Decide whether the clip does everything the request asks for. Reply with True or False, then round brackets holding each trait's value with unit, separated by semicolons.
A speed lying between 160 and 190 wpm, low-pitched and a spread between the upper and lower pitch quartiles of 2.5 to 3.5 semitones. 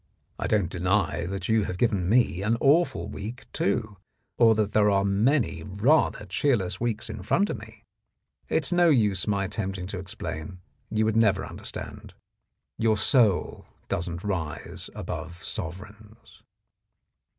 False (140 wpm; 105 Hz; 3.1 semitones)